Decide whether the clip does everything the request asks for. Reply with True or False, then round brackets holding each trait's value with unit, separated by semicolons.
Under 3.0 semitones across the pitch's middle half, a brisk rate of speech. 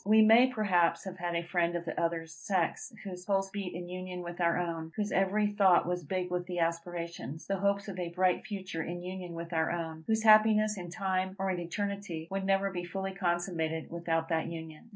True (2.5 semitones; 215 wpm)